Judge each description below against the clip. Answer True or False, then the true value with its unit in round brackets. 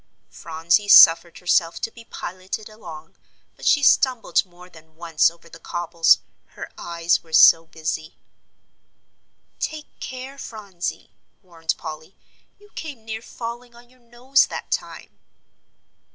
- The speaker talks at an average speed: False (130 wpm)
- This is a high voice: False (180 Hz)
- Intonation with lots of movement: True (6.2 semitones)